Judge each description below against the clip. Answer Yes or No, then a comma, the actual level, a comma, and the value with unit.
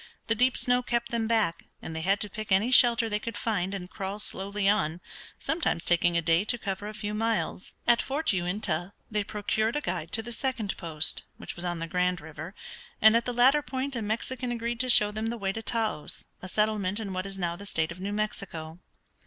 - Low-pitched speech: No, high, 210 Hz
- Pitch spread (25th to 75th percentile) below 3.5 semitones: No, average, 4.1 semitones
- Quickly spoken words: Yes, fast, 225 wpm